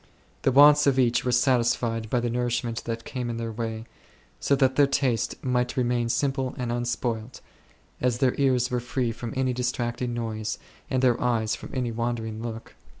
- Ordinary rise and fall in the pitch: No, narrow, 1.7 semitones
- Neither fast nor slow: Yes, average, 180 wpm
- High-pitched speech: No, low, 120 Hz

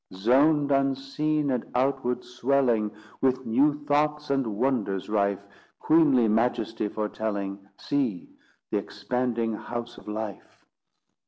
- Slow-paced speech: Yes, slow, 105 wpm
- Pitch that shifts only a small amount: No, average, 4.3 semitones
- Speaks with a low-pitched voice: Yes, low, 125 Hz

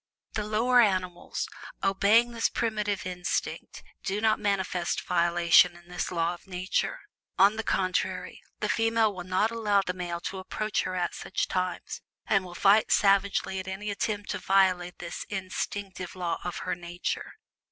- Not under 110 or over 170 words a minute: Yes, average, 160 wpm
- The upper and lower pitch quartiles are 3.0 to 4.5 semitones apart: No, narrow, 2.6 semitones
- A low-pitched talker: No, high, 190 Hz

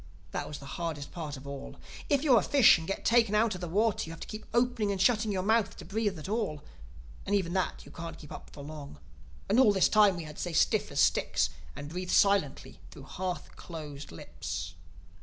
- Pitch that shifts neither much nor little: No, wide, 6.1 semitones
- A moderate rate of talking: No, fast, 225 wpm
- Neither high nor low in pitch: Yes, medium, 180 Hz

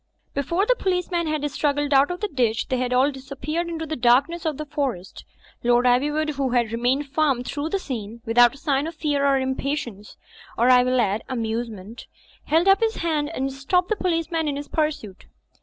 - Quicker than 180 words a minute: Yes, average, 195 wpm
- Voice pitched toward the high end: Yes, very high, 280 Hz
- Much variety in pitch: No, average, 4.2 semitones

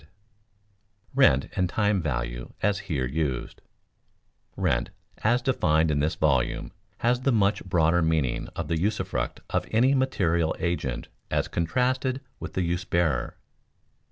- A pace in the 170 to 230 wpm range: No, slow, 135 wpm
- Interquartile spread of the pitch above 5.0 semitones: Yes, wide, 5.6 semitones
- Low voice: Yes, very low, 85 Hz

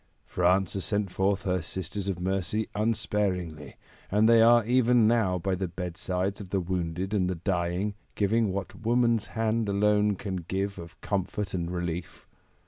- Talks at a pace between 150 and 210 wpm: Yes, average, 160 wpm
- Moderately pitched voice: No, very low, 95 Hz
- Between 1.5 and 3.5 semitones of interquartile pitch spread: Yes, narrow, 2.6 semitones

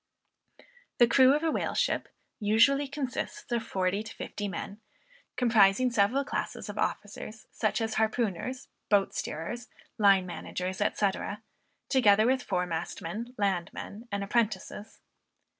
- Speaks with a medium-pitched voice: No, high, 215 Hz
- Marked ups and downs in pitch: No, average, 3.7 semitones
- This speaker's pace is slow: Yes, slow, 125 wpm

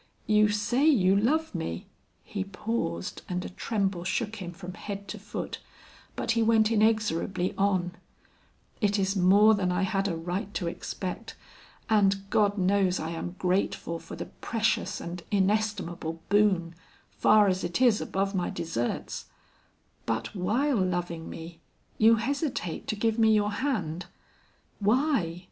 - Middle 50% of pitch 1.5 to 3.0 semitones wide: No, average, 3.4 semitones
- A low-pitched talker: No, high, 195 Hz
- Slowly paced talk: No, average, 150 wpm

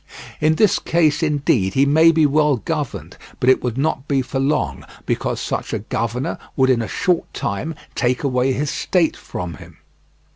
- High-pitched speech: No, medium, 140 Hz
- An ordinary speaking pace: Yes, average, 180 wpm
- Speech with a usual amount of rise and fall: Yes, average, 3.8 semitones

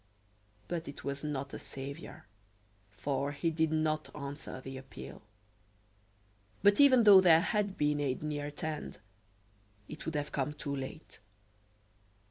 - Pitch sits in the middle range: Yes, medium, 150 Hz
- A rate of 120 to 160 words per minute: Yes, average, 140 wpm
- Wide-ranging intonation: No, narrow, 2.5 semitones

